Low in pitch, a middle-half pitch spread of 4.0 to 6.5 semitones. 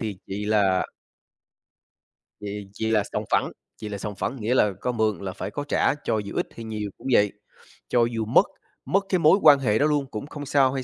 Yes: low, 110 Hz; average, 4.7 semitones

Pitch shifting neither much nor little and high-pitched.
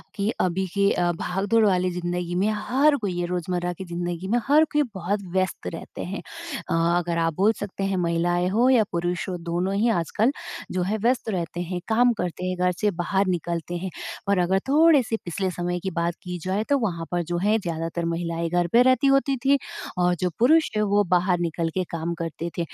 No: average, 3.2 semitones; medium, 180 Hz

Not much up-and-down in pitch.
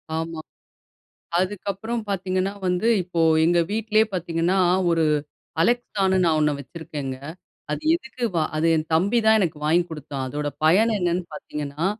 No: average, 4.0 semitones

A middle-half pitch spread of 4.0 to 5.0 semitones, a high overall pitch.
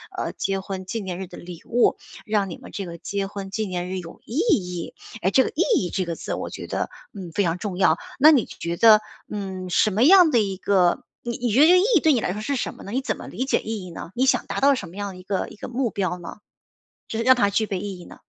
Yes: average, 4.6 semitones; high, 200 Hz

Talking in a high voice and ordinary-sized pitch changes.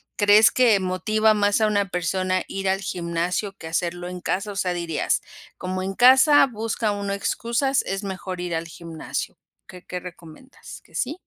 Yes: high, 195 Hz; average, 3.2 semitones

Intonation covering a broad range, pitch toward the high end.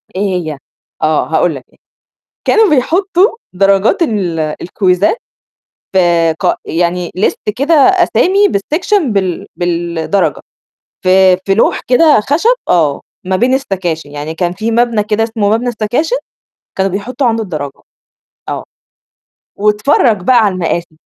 Yes: wide, 6.4 semitones; high, 200 Hz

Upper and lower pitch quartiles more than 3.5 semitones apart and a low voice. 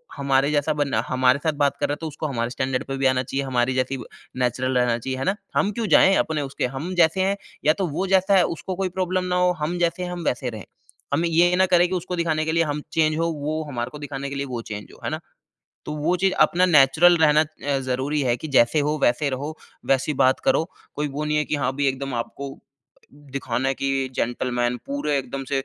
No: average, 4.2 semitones; medium, 145 Hz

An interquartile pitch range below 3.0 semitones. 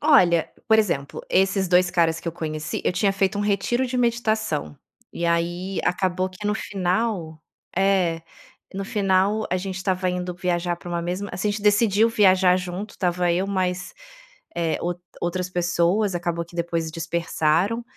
Yes: narrow, 2.6 semitones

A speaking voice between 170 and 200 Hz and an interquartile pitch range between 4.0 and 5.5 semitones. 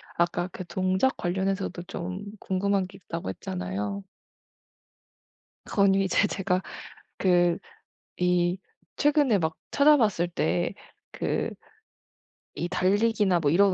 No: medium, 185 Hz; narrow, 2.4 semitones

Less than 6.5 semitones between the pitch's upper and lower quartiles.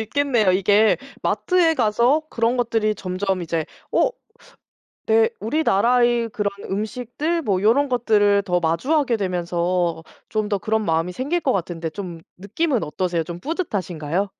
Yes: average, 5.2 semitones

